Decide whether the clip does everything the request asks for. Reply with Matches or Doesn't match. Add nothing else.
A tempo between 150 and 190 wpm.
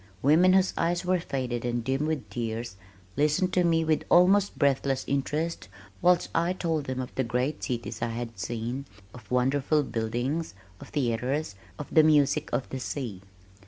Matches